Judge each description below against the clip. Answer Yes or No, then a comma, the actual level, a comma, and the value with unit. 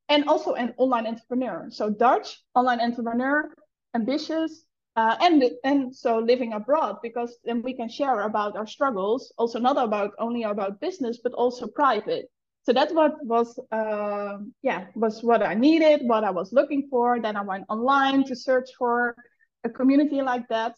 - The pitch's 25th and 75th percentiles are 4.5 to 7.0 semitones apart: No, average, 3.3 semitones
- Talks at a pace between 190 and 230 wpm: No, average, 170 wpm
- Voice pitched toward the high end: Yes, high, 245 Hz